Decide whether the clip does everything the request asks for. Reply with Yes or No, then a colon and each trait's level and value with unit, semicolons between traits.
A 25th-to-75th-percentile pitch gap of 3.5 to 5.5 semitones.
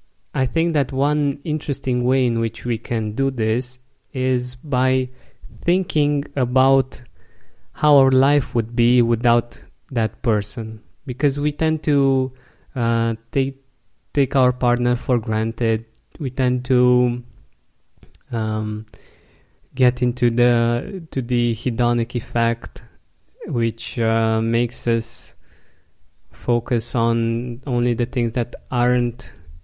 No: narrow, 2.5 semitones